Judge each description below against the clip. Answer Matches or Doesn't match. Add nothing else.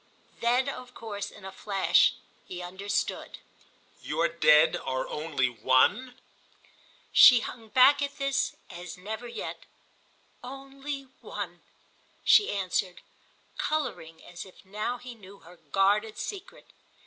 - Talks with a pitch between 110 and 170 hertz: Doesn't match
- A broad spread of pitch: Matches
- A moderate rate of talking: Doesn't match